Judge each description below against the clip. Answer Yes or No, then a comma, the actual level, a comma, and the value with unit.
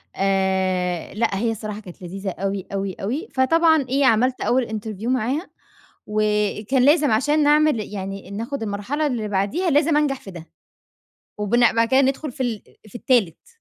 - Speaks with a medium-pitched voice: No, high, 225 Hz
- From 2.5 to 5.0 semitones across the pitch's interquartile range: No, wide, 5.6 semitones